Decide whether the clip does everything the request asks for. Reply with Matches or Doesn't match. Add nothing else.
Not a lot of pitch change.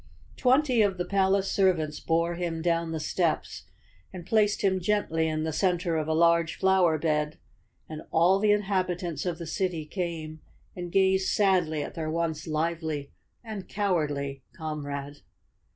Doesn't match